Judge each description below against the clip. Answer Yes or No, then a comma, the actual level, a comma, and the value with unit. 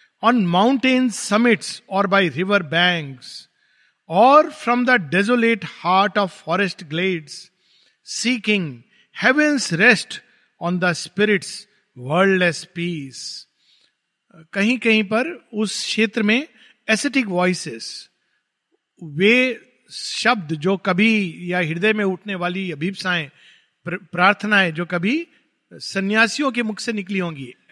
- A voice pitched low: No, high, 195 Hz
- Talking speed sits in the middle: No, slow, 105 wpm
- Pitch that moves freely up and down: No, average, 4.6 semitones